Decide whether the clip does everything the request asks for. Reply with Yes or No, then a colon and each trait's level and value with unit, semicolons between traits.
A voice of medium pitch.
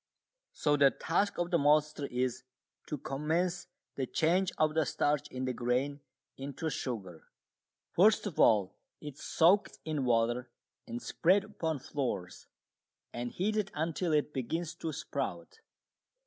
Yes: medium, 150 Hz